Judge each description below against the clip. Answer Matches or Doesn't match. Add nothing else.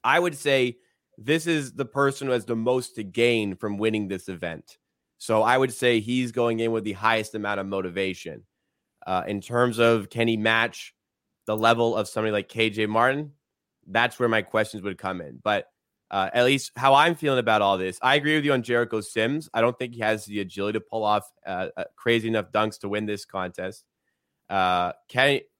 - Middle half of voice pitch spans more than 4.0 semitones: Doesn't match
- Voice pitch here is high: Doesn't match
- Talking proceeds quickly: Matches